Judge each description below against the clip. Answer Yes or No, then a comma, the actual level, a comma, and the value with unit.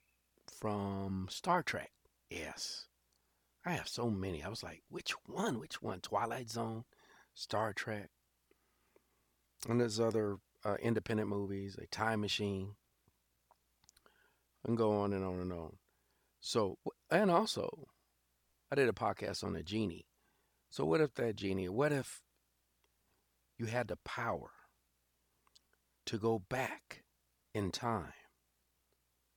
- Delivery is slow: Yes, slow, 125 wpm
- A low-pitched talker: Yes, very low, 95 Hz